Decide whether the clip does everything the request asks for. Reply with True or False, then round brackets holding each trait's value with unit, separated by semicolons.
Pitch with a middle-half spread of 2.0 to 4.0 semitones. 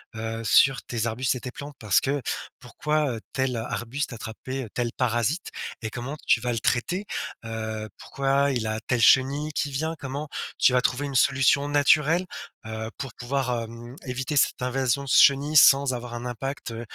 True (3.0 semitones)